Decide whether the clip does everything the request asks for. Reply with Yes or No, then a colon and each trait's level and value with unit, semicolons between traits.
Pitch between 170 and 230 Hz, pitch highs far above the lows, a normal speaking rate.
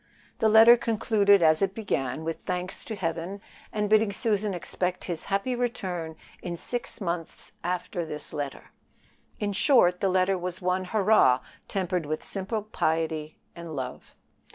No: medium, 185 Hz; average, 4.0 semitones; average, 150 wpm